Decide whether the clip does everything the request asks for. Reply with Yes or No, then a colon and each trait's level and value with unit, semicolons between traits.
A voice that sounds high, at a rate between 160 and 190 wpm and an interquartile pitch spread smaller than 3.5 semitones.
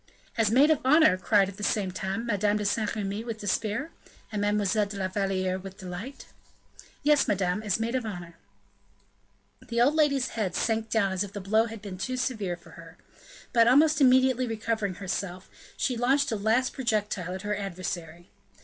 No: high, 210 Hz; average, 185 wpm; average, 3.8 semitones